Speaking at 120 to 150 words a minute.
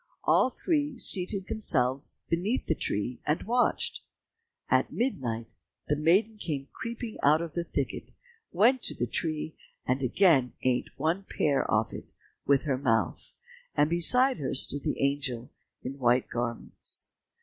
Yes: average, 145 wpm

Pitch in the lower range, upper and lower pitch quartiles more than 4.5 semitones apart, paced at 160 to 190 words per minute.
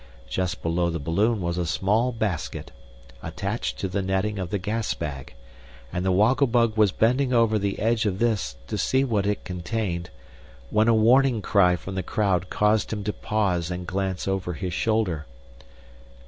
No: low, 100 Hz; average, 3.6 semitones; average, 175 wpm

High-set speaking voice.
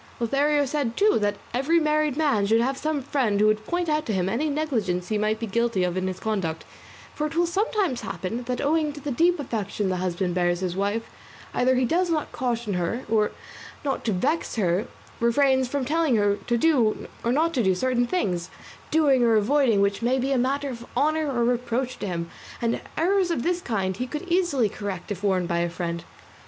Yes: high, 240 Hz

